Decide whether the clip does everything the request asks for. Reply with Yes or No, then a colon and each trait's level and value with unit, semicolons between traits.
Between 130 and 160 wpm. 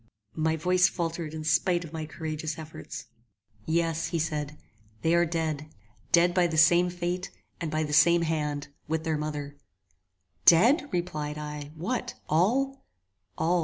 Yes: average, 150 wpm